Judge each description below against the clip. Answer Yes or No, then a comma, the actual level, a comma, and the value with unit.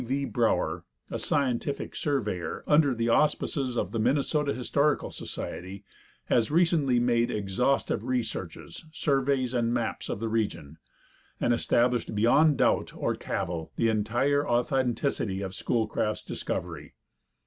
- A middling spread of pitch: Yes, average, 3.9 semitones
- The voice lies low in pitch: Yes, low, 120 Hz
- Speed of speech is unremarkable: No, slow, 125 wpm